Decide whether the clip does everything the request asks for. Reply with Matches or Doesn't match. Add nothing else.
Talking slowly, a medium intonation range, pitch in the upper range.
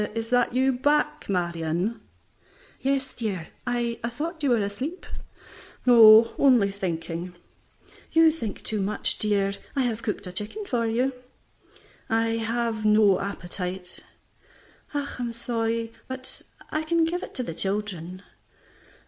Matches